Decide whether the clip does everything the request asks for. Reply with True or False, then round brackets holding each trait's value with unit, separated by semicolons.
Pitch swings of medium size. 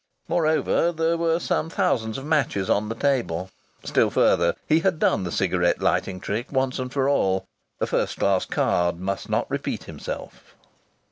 False (8.7 semitones)